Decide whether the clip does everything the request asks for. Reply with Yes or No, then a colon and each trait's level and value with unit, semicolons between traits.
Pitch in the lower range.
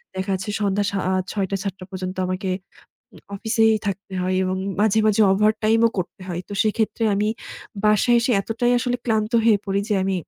No: high, 205 Hz